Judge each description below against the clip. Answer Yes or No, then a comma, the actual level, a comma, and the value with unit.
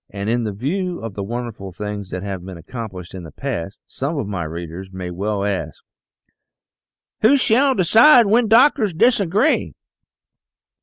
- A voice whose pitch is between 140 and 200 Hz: No, low, 110 Hz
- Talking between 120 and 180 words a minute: Yes, average, 150 wpm